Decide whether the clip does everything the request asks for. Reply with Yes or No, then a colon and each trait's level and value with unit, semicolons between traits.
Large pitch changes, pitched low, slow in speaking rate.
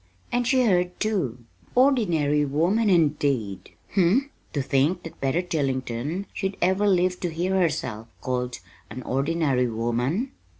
No: wide, 6.3 semitones; medium, 165 Hz; slow, 130 wpm